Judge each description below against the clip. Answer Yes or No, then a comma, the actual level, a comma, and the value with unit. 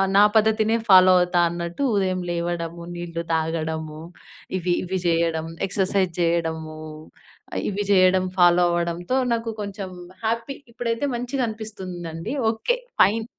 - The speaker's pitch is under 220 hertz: Yes, medium, 185 Hz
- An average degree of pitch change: Yes, average, 4.1 semitones